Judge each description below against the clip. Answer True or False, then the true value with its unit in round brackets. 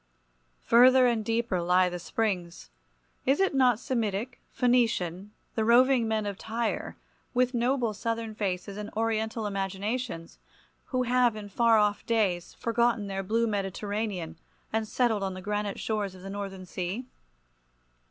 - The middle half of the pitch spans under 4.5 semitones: True (3.3 semitones)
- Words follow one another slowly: False (145 wpm)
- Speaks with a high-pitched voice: True (215 Hz)